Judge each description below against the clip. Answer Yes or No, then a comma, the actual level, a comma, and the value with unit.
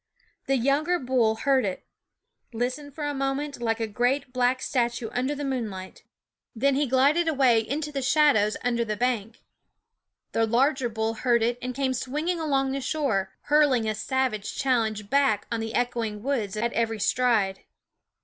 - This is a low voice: No, very high, 250 Hz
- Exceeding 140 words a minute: Yes, average, 165 wpm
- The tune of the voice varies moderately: Yes, average, 3.6 semitones